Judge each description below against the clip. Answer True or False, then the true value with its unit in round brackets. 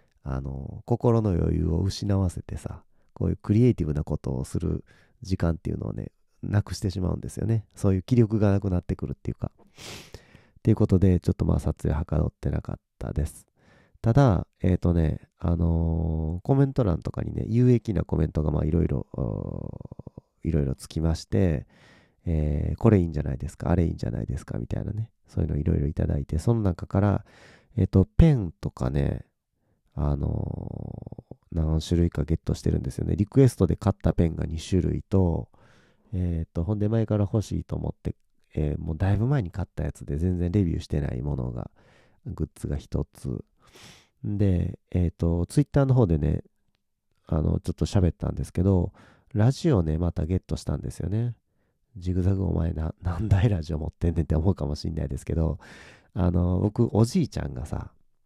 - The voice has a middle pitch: False (90 Hz)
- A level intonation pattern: False (4.9 semitones)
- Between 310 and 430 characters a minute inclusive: True (370 characters per minute)